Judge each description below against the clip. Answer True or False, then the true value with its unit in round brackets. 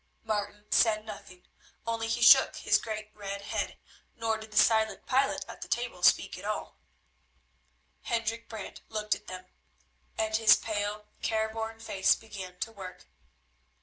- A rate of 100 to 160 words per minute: True (150 wpm)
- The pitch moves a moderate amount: False (1.4 semitones)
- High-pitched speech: True (220 Hz)